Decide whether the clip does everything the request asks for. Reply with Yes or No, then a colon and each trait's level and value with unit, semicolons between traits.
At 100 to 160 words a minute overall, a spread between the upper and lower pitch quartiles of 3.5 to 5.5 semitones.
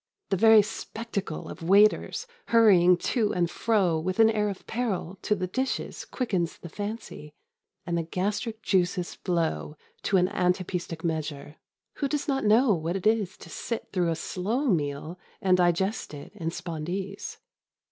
Yes: average, 155 wpm; average, 4.0 semitones